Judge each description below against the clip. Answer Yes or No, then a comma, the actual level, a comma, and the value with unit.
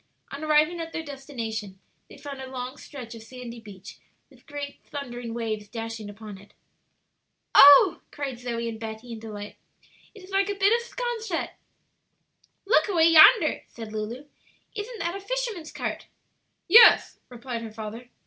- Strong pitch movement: Yes, wide, 6.7 semitones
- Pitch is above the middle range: Yes, very high, 255 Hz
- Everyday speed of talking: Yes, average, 160 wpm